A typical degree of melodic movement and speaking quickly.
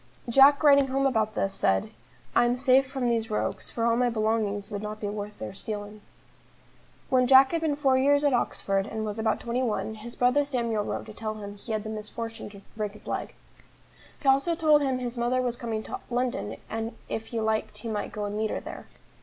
Yes: average, 3.5 semitones; fast, 225 wpm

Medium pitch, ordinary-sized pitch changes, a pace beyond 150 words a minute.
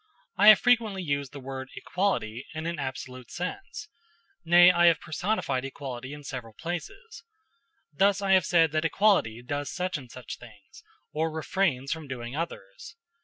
No: medium, 155 Hz; wide, 6.0 semitones; average, 160 wpm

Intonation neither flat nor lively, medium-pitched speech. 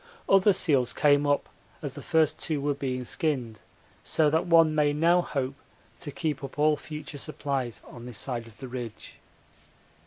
Yes: average, 3.3 semitones; medium, 145 Hz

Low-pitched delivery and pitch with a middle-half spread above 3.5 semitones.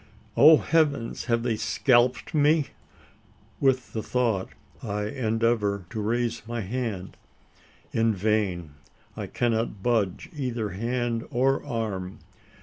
No: low, 115 Hz; average, 3.2 semitones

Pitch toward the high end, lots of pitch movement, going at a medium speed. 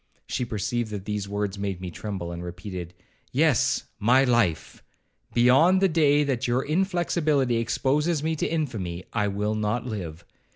No: low, 115 Hz; wide, 6.3 semitones; average, 155 wpm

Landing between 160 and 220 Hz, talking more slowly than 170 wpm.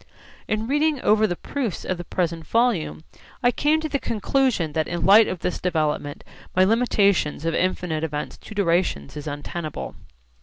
No: medium, 185 Hz; average, 175 wpm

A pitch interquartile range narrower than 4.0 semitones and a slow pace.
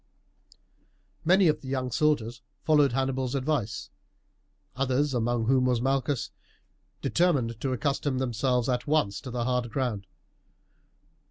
Yes: narrow, 2.5 semitones; slow, 120 wpm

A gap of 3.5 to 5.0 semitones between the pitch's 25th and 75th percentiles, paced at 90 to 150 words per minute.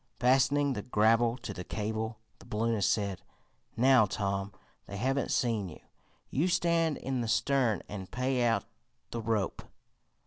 Yes: average, 3.9 semitones; average, 145 wpm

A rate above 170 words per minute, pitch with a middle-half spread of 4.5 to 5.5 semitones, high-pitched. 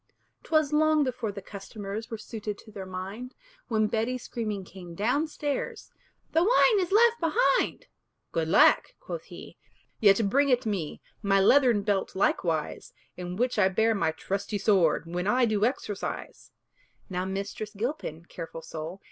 No: average, 155 wpm; average, 4.9 semitones; high, 210 Hz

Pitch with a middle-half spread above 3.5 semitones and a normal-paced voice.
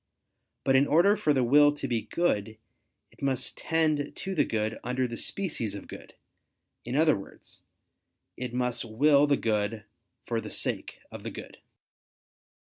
Yes: average, 4.6 semitones; average, 160 wpm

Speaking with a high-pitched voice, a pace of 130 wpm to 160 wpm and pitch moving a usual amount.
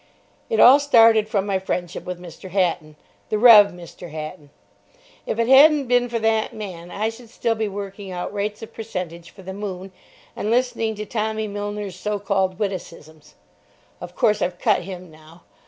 No: high, 205 Hz; average, 175 wpm; average, 3.5 semitones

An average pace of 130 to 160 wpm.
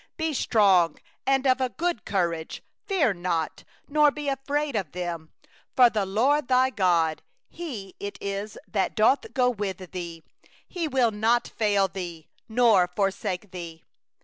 Yes: average, 145 wpm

